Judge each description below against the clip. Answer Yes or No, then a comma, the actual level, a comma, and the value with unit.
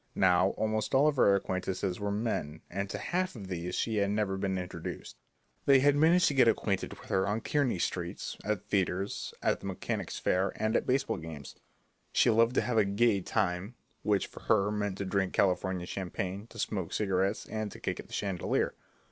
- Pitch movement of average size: Yes, average, 3.1 semitones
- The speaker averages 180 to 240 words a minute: Yes, average, 200 wpm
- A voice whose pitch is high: No, low, 100 Hz